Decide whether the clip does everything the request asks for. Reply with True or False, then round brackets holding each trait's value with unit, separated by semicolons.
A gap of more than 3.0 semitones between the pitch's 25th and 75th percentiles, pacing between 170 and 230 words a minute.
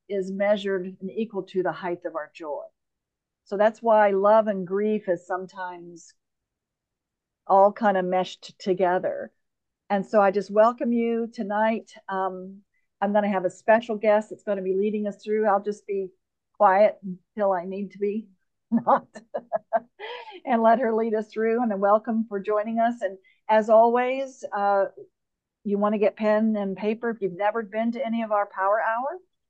False (2.6 semitones; 180 wpm)